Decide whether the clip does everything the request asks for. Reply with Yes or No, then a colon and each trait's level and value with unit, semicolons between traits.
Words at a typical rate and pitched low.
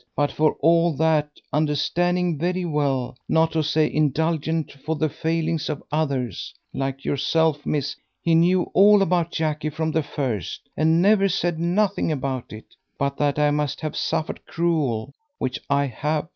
No: average, 160 wpm; medium, 155 Hz